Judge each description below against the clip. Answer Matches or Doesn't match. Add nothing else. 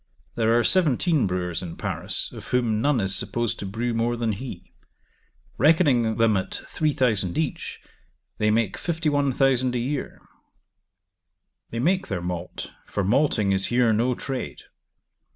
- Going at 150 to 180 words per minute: Doesn't match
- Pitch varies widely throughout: Doesn't match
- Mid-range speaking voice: Doesn't match